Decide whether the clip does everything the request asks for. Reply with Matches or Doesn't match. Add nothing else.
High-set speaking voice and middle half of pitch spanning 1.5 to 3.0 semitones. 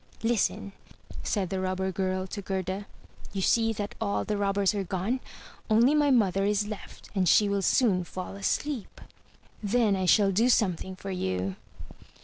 Matches